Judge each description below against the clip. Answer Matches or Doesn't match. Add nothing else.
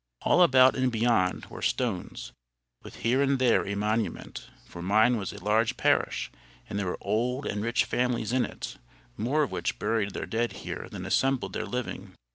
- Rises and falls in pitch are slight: Doesn't match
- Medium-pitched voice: Doesn't match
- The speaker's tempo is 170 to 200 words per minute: Matches